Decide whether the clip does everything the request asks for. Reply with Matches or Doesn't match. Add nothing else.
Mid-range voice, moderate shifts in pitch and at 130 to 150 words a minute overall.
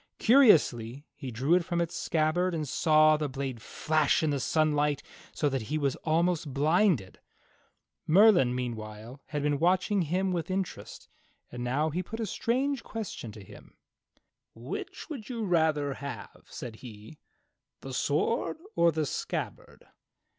Matches